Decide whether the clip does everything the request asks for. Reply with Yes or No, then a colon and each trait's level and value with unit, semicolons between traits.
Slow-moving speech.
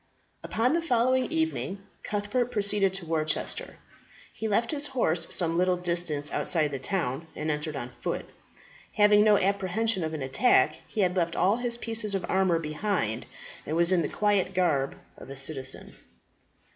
No: average, 165 wpm